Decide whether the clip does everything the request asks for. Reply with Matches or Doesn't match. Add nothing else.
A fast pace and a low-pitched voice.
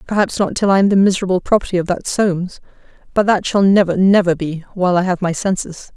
Doesn't match